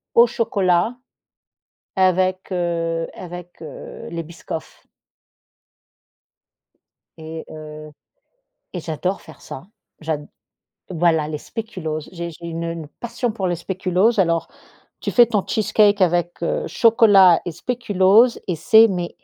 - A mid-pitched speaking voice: Yes, medium, 175 Hz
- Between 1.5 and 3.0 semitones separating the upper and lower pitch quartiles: No, average, 3.4 semitones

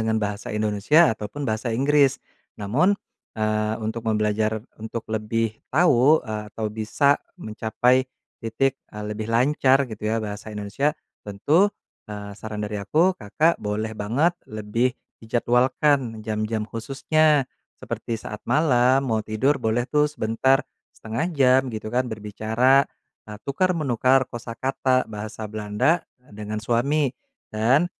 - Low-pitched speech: Yes, low, 115 Hz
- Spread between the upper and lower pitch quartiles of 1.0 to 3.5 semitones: No, average, 4.0 semitones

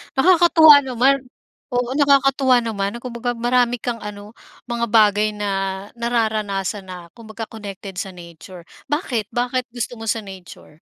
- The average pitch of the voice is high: Yes, high, 230 Hz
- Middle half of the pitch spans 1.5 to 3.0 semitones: No, average, 3.5 semitones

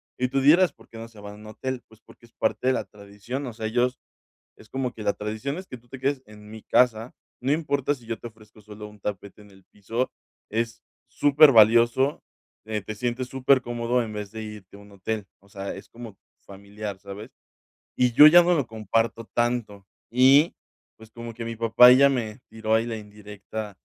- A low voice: Yes, low, 115 Hz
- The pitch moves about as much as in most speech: Yes, average, 3.1 semitones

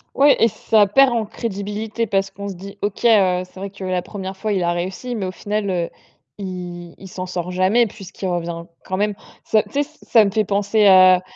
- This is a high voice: Yes, high, 195 Hz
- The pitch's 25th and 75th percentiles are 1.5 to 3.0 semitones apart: Yes, narrow, 2.5 semitones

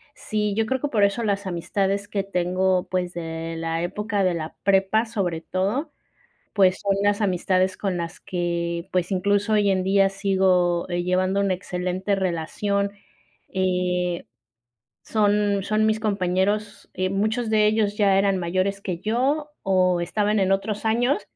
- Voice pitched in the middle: No, high, 195 Hz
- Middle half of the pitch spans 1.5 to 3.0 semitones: Yes, narrow, 2.4 semitones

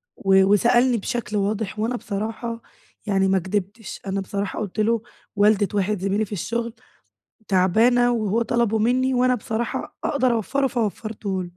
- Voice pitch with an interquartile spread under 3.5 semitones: Yes, average, 3.0 semitones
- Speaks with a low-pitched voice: No, high, 215 Hz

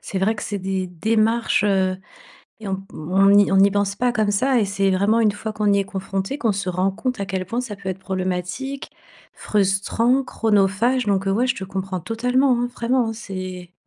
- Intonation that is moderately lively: Yes, average, 3.0 semitones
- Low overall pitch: No, high, 200 Hz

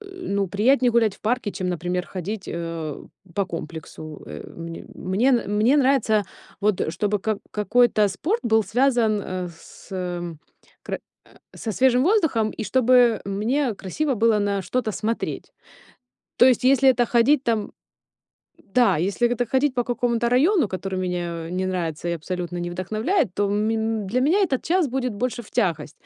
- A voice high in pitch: Yes, high, 215 Hz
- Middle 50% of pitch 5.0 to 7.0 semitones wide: Yes, average, 5.3 semitones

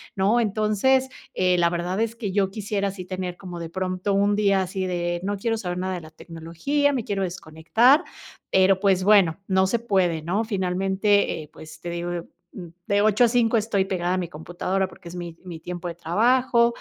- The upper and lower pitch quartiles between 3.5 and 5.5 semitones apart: No, average, 3.0 semitones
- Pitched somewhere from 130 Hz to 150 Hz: No, high, 190 Hz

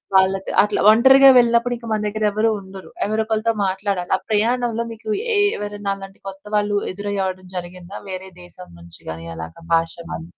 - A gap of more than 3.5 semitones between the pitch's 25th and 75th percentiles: No, average, 2.9 semitones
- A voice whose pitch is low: No, high, 205 Hz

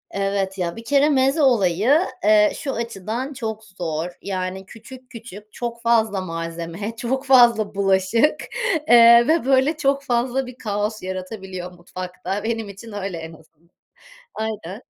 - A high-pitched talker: Yes, high, 215 Hz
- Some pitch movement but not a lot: Yes, average, 4.3 semitones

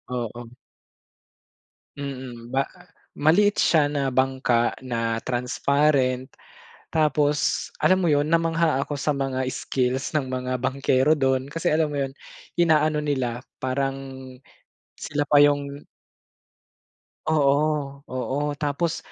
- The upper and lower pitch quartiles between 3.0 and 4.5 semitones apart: No, narrow, 2.5 semitones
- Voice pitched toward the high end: No, medium, 140 Hz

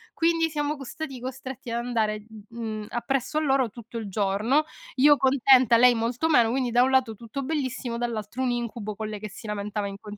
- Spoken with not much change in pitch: No, average, 3.7 semitones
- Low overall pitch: No, high, 240 Hz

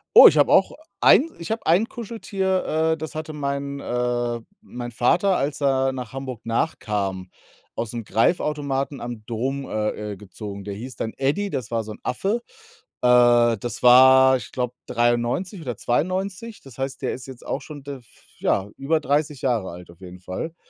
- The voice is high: No, low, 130 Hz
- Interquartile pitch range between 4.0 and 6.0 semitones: Yes, average, 4.4 semitones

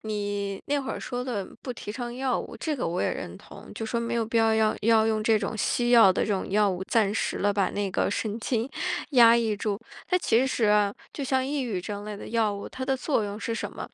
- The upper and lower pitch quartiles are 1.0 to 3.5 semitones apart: Yes, average, 2.9 semitones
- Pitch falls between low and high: No, high, 220 Hz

